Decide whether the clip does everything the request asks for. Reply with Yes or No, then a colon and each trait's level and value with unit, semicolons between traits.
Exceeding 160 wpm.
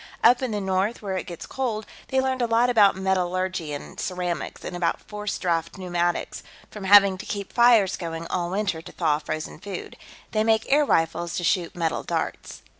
Yes: average, 190 wpm